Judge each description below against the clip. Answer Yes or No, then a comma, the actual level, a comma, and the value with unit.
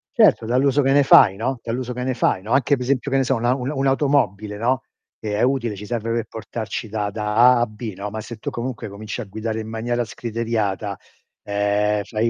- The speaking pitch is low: Yes, low, 115 Hz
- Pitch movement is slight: No, average, 3.1 semitones